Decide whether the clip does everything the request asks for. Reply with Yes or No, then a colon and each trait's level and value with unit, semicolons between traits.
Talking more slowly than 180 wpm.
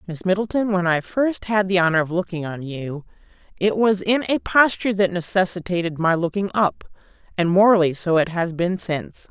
No: average, 185 wpm